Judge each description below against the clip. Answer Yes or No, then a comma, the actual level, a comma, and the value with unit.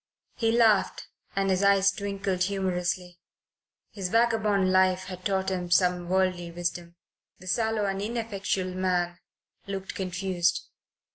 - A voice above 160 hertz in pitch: Yes, high, 190 Hz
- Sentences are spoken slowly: Yes, slow, 125 wpm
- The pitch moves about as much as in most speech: No, narrow, 1.8 semitones